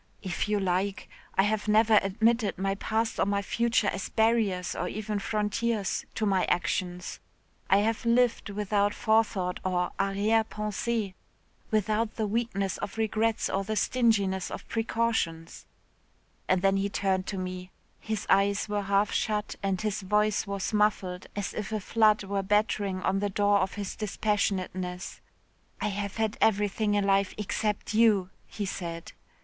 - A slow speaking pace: No, average, 155 wpm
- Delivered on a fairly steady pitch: Yes, narrow, 2.0 semitones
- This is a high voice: Yes, high, 205 Hz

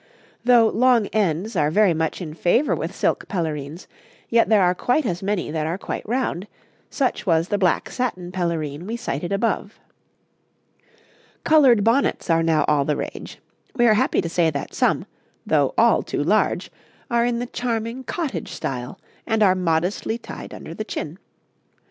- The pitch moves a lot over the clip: Yes, wide, 6.2 semitones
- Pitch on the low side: No, high, 195 Hz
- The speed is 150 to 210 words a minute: Yes, average, 165 wpm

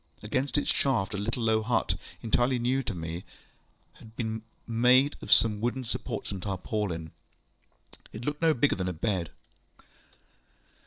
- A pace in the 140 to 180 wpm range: Yes, average, 150 wpm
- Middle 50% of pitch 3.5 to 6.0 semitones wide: Yes, average, 4.1 semitones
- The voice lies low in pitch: Yes, low, 110 Hz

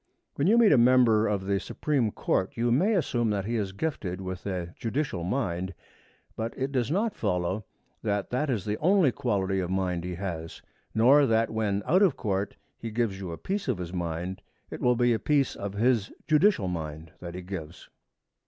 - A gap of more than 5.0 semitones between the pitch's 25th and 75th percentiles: Yes, wide, 5.5 semitones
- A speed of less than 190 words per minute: No, average, 200 wpm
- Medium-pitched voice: No, low, 105 Hz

